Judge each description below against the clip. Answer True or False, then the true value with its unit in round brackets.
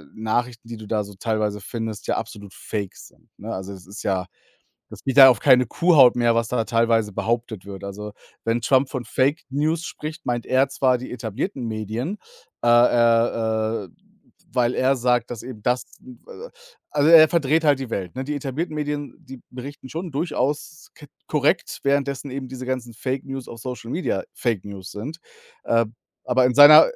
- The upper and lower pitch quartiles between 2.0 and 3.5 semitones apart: False (3.9 semitones)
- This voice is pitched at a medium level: False (125 Hz)